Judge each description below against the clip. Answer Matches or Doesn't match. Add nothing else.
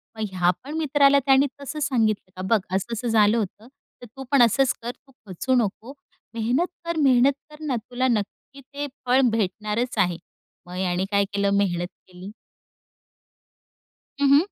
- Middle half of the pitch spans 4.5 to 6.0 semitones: Matches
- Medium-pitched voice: Doesn't match